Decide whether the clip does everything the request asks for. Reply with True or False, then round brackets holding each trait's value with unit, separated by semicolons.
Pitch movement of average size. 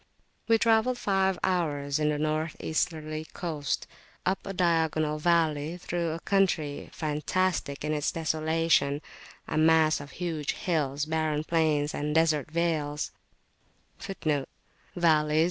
False (2.2 semitones)